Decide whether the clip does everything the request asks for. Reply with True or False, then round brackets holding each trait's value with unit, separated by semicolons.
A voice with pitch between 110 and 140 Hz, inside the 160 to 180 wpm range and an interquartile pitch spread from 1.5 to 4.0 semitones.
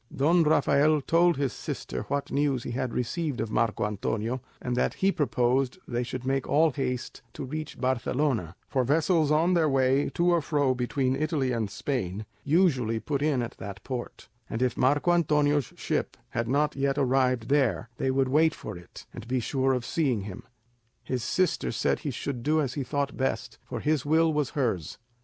False (135 Hz; 190 wpm; 3.4 semitones)